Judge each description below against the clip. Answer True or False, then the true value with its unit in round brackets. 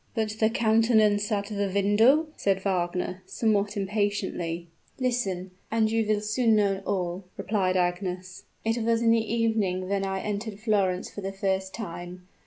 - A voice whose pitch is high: True (205 Hz)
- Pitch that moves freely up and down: False (2.7 semitones)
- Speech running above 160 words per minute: False (155 wpm)